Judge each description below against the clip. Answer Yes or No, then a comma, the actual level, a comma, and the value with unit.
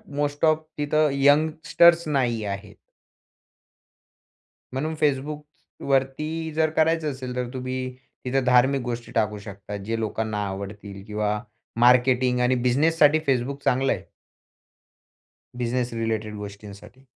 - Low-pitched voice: Yes, low, 130 Hz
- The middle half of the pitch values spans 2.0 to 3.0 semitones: No, average, 4.9 semitones